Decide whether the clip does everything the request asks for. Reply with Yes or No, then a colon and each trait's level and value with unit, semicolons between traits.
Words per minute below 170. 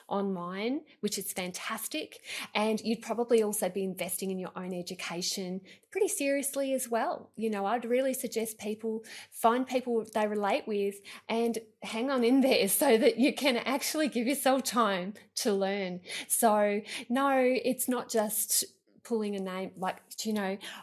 Yes: average, 160 wpm